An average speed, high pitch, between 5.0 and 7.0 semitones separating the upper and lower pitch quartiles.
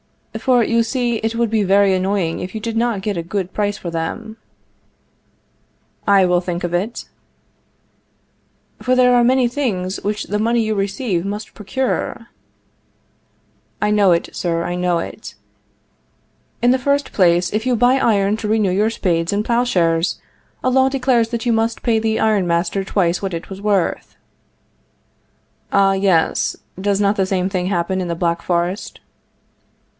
No: average, 165 wpm; high, 205 Hz; average, 4.0 semitones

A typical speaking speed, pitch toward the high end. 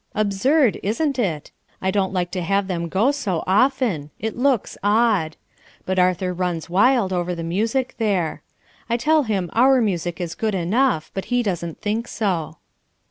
Yes: average, 165 wpm; high, 195 Hz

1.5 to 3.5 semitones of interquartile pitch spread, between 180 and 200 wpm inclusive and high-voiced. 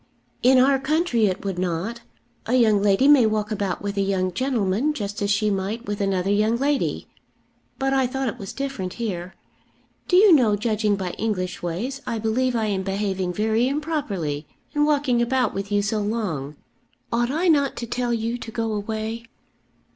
No: average, 4.3 semitones; average, 185 wpm; high, 220 Hz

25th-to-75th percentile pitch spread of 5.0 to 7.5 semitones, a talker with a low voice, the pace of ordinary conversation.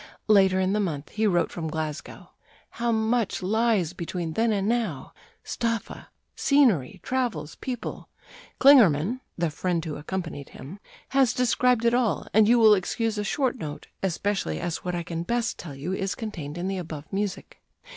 No: wide, 5.6 semitones; high, 195 Hz; average, 165 wpm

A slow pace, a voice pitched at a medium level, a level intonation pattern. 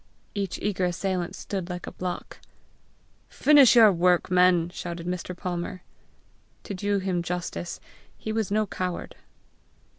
Yes: slow, 130 wpm; medium, 180 Hz; narrow, 2.2 semitones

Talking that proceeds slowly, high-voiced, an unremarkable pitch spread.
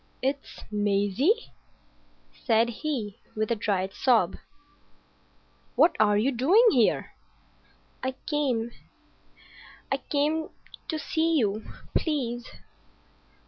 No: slow, 85 wpm; high, 245 Hz; wide, 5.9 semitones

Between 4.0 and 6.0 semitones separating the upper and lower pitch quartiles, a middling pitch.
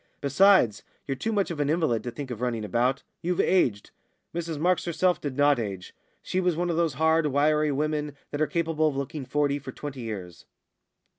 Yes: average, 4.3 semitones; medium, 145 Hz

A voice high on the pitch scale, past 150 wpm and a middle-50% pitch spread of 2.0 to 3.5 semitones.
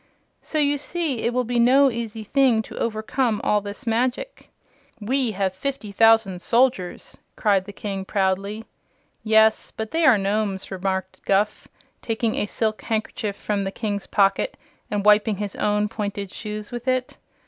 Yes: high, 215 Hz; average, 160 wpm; average, 3.0 semitones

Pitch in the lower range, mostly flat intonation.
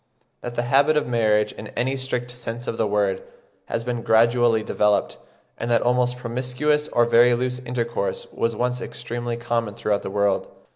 Yes: low, 120 Hz; narrow, 1.5 semitones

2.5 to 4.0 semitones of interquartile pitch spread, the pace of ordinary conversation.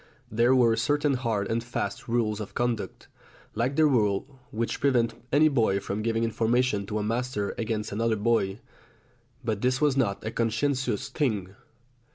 Yes: average, 2.9 semitones; average, 160 wpm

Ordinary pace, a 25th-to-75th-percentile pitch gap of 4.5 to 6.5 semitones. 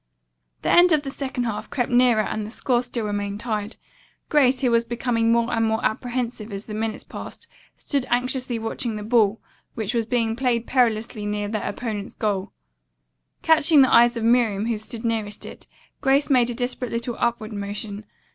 No: average, 185 wpm; narrow, 2.5 semitones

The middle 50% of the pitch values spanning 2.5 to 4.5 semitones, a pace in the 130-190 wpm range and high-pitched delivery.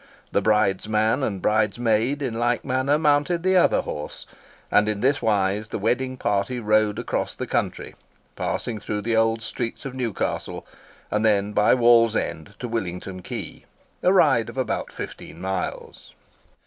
No: average, 3.5 semitones; average, 150 wpm; low, 115 Hz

